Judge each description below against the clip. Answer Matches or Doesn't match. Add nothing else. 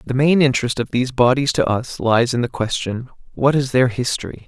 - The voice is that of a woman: Doesn't match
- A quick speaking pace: Matches